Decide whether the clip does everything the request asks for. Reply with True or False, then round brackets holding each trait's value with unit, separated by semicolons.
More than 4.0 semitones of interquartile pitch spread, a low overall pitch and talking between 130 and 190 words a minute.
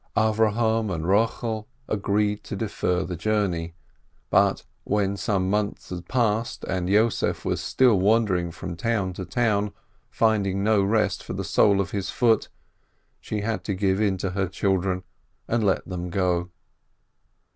False (2.8 semitones; 100 Hz; 150 wpm)